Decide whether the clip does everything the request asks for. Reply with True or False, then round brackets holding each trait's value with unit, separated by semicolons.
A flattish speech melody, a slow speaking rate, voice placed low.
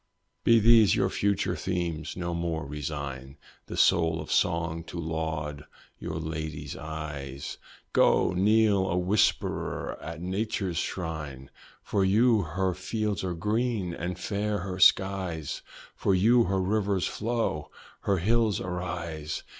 False (4.0 semitones; 130 wpm; 90 Hz)